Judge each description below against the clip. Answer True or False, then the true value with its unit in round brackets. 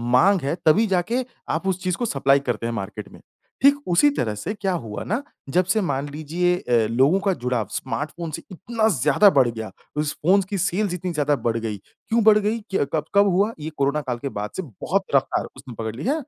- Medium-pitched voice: True (155 Hz)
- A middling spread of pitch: False (7.3 semitones)